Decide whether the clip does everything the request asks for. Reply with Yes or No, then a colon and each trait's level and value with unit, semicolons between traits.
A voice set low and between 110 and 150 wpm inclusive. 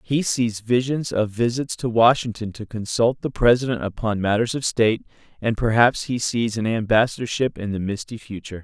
No: low, 115 Hz; average, 175 wpm